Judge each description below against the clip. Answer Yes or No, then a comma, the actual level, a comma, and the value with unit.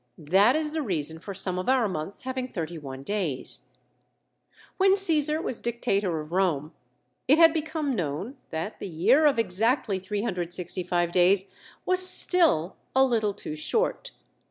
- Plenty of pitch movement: Yes, wide, 7.6 semitones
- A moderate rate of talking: Yes, average, 150 wpm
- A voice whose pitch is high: Yes, high, 200 Hz